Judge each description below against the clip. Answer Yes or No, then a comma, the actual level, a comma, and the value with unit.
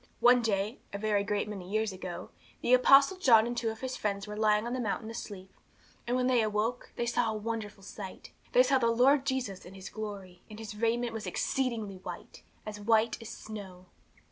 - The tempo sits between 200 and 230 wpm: Yes, fast, 205 wpm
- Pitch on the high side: Yes, high, 220 Hz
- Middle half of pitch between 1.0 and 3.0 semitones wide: Yes, average, 2.7 semitones